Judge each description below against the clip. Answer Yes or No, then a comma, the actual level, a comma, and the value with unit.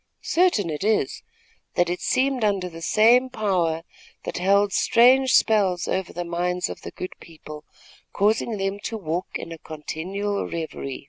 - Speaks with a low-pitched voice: No, high, 190 Hz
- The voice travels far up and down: No, average, 4.3 semitones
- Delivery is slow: No, average, 155 wpm